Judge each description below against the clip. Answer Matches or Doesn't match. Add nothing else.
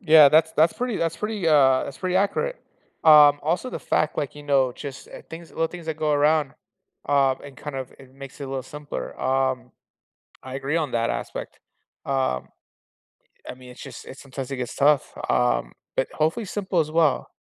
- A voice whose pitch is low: Doesn't match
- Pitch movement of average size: Matches